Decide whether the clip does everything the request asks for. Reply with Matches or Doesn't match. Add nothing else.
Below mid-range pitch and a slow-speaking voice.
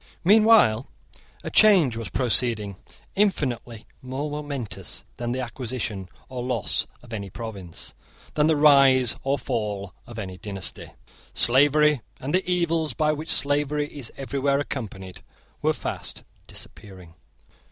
Matches